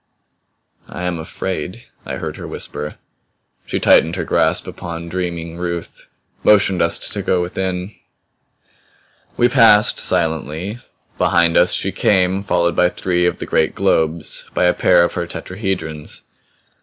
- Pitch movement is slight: Yes, narrow, 2.0 semitones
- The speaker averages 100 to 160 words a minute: Yes, average, 140 wpm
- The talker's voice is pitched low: Yes, very low, 90 Hz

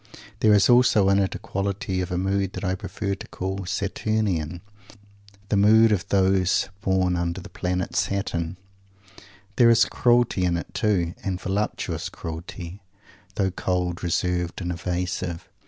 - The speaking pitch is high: No, very low, 95 Hz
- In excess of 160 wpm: No, average, 145 wpm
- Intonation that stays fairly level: Yes, narrow, 2.1 semitones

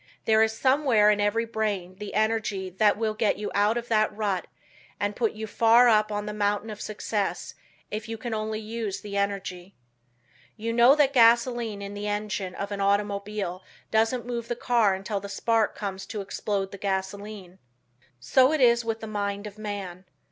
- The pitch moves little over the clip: Yes, narrow, 2.0 semitones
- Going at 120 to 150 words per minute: No, average, 185 wpm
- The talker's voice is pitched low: No, high, 210 Hz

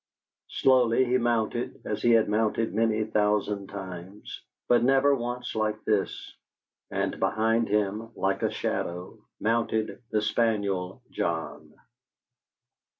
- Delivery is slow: Yes, slow, 115 wpm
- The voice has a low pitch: Yes, low, 110 Hz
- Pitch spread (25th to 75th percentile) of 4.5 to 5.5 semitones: No, average, 2.7 semitones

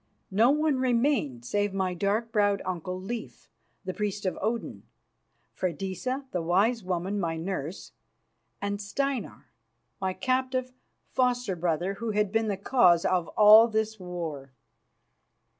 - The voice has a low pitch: No, high, 200 Hz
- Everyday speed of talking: No, slow, 130 wpm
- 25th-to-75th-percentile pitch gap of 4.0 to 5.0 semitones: Yes, average, 4.3 semitones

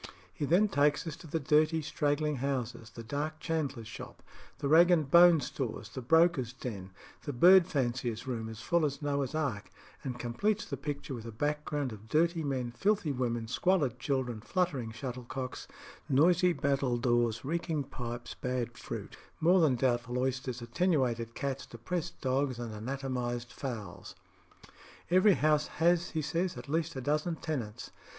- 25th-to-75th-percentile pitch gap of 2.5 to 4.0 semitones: No, average, 4.7 semitones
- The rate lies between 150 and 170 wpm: Yes, average, 155 wpm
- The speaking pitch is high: No, low, 135 Hz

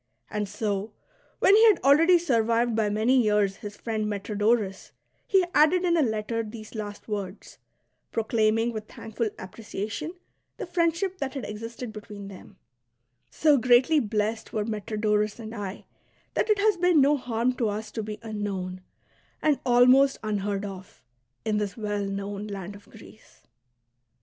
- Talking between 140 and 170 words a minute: Yes, average, 155 wpm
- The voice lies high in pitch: Yes, high, 220 Hz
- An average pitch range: Yes, average, 3.5 semitones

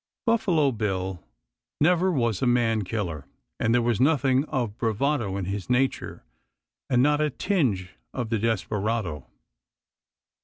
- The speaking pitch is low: Yes, low, 115 Hz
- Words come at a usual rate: No, slow, 130 wpm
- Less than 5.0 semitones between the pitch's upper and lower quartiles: No, average, 5.3 semitones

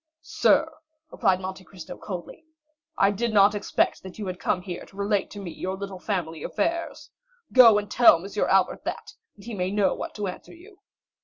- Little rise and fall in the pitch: Yes, narrow, 2.2 semitones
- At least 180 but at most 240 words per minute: Yes, average, 190 wpm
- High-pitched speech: Yes, high, 200 Hz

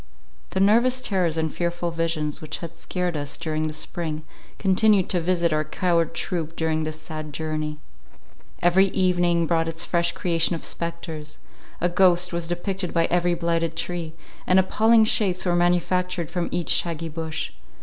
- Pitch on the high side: No, medium, 170 Hz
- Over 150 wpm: Yes, average, 160 wpm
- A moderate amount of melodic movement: No, narrow, 2.0 semitones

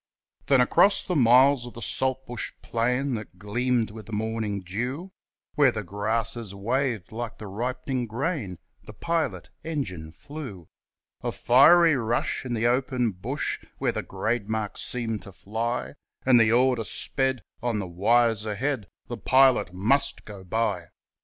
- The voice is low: Yes, low, 120 Hz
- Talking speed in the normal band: Yes, average, 150 wpm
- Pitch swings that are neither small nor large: Yes, average, 3.7 semitones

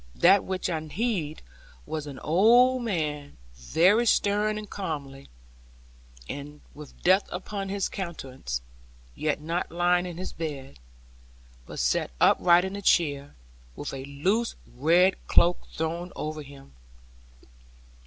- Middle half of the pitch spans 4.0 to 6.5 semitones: Yes, average, 4.6 semitones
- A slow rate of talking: Yes, slow, 125 wpm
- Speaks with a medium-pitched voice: Yes, medium, 170 Hz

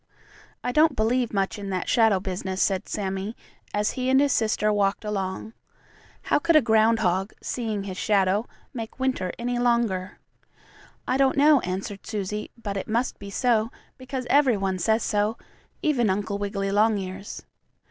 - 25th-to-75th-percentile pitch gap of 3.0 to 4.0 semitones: Yes, average, 3.6 semitones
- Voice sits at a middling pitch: No, high, 215 Hz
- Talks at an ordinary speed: Yes, average, 160 wpm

